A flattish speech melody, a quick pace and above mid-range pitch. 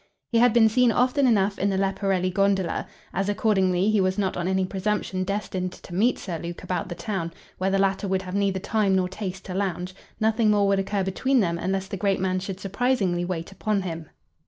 Yes: narrow, 1.9 semitones; fast, 215 wpm; high, 195 Hz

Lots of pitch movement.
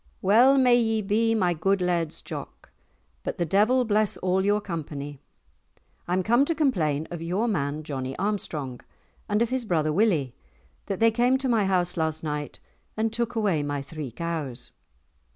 Yes: wide, 6.4 semitones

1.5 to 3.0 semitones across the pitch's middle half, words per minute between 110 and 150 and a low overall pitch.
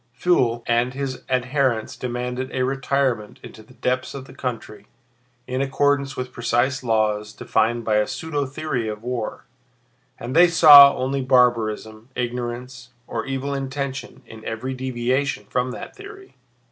Yes: narrow, 2.6 semitones; average, 145 wpm; low, 125 Hz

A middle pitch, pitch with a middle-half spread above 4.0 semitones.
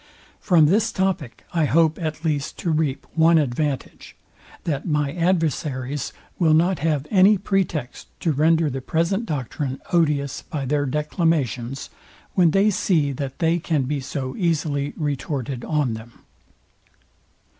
No: medium, 150 Hz; average, 3.2 semitones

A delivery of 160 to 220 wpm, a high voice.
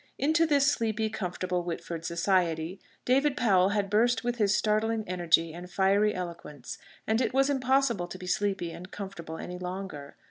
Yes: average, 165 wpm; high, 195 Hz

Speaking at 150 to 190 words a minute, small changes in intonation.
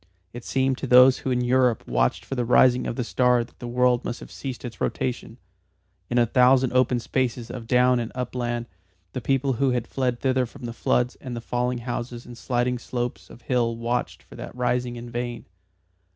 No: fast, 205 wpm; narrow, 1.1 semitones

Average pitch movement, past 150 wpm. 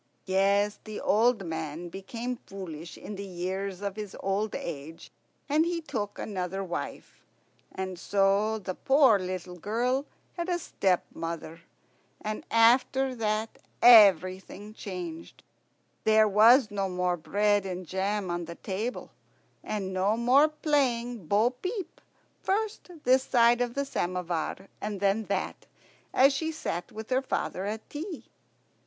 No: average, 4.6 semitones; slow, 135 wpm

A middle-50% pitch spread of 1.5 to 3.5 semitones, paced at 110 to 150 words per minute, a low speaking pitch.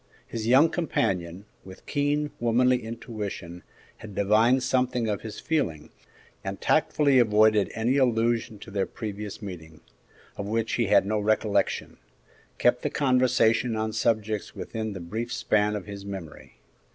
Yes: average, 3.1 semitones; average, 140 wpm; low, 110 Hz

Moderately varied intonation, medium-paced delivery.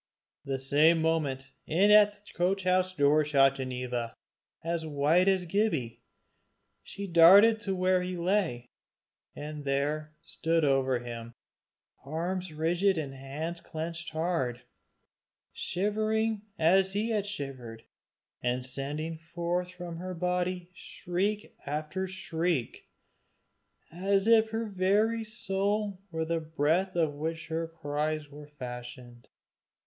No: average, 4.7 semitones; slow, 120 wpm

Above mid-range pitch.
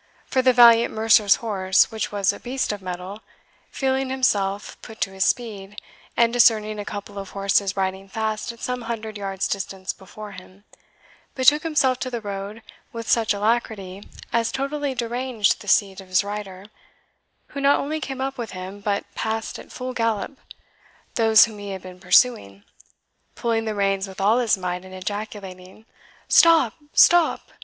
Yes: high, 215 Hz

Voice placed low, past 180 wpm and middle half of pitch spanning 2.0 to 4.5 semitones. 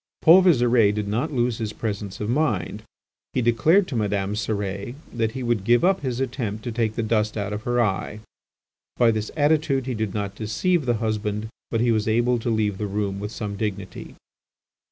Yes: low, 110 Hz; average, 195 wpm; average, 2.7 semitones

